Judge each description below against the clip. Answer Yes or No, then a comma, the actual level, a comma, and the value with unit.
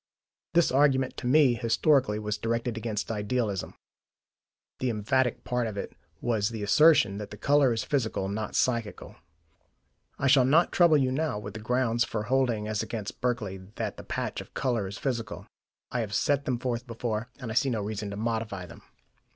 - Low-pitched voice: Yes, low, 115 Hz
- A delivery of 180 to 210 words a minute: Yes, average, 185 wpm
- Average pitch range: Yes, average, 3.6 semitones